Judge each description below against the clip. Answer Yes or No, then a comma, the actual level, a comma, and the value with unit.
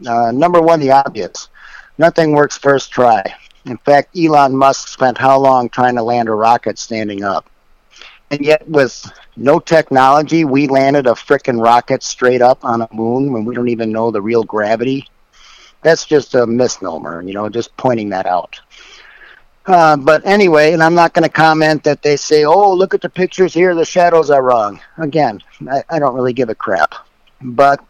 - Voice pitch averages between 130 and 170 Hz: Yes, low, 135 Hz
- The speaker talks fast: No, average, 185 wpm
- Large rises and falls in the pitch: No, average, 4.5 semitones